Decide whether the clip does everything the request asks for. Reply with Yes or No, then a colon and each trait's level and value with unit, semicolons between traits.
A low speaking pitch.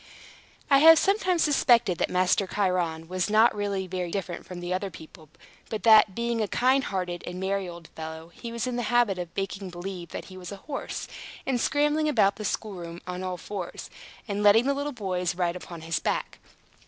No: high, 195 Hz